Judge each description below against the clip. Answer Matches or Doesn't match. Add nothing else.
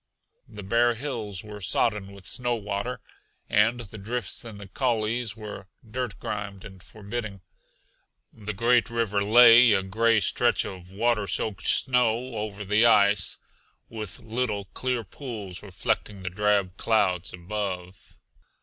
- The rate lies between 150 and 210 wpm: Doesn't match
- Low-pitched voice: Matches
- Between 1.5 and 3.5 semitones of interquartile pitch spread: Matches